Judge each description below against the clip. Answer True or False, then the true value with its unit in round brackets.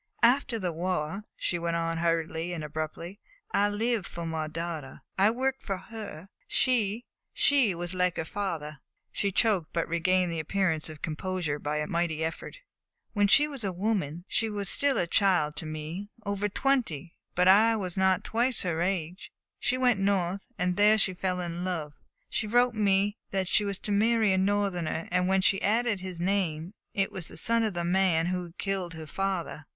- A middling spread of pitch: True (3.6 semitones)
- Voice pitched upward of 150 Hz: True (185 Hz)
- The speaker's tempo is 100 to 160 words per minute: False (190 wpm)